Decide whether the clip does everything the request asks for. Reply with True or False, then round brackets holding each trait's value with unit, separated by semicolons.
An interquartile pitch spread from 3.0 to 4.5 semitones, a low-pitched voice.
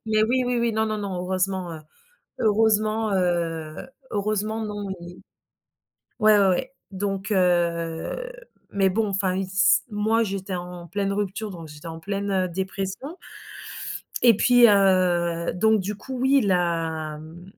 False (3.4 semitones; 195 Hz)